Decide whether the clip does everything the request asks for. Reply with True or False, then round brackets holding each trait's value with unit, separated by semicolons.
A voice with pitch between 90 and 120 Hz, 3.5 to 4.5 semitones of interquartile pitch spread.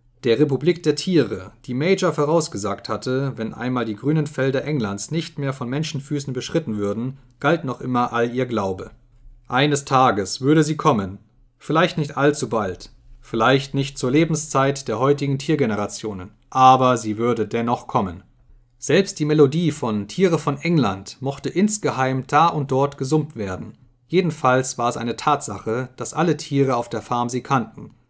False (130 Hz; 3.9 semitones)